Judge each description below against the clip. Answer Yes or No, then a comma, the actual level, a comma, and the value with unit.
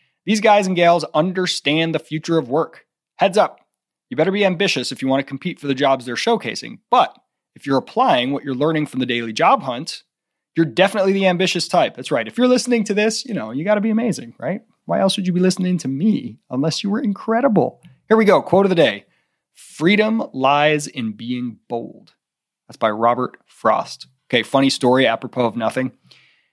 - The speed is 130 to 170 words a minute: No, fast, 205 wpm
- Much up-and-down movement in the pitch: Yes, wide, 7.0 semitones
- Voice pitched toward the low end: No, medium, 160 Hz